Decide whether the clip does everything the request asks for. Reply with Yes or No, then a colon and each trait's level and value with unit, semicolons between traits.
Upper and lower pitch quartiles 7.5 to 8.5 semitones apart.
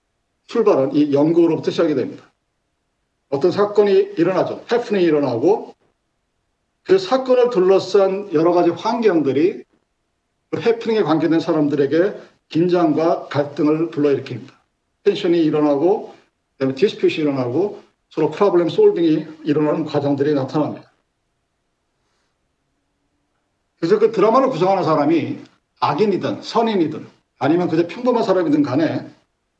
No: wide, 6.3 semitones